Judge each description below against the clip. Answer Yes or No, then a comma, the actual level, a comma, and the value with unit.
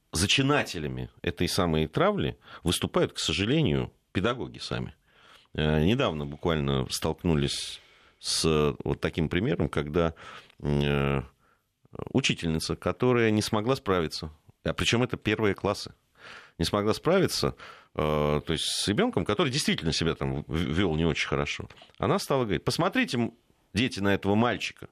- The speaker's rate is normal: Yes, average, 120 wpm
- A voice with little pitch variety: No, average, 5.2 semitones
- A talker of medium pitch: No, very low, 85 Hz